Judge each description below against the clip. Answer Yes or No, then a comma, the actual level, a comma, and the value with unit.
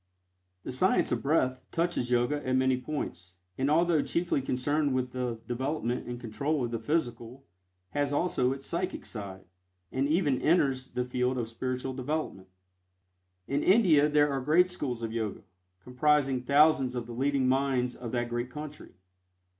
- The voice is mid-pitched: No, low, 130 Hz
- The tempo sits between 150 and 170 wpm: Yes, average, 160 wpm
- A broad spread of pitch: No, average, 3.2 semitones